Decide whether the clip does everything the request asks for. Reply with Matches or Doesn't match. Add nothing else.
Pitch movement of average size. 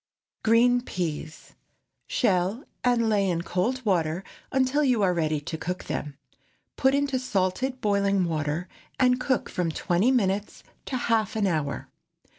Doesn't match